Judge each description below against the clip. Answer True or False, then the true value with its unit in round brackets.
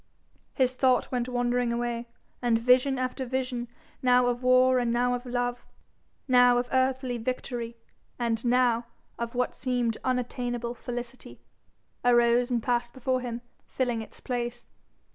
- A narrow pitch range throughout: True (1.0 semitones)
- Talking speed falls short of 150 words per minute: True (140 wpm)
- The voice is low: False (245 Hz)